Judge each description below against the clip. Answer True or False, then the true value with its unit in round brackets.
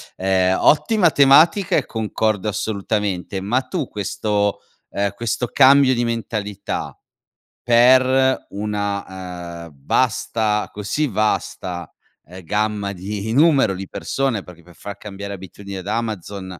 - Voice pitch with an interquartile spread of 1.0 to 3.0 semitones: False (3.7 semitones)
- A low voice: True (105 Hz)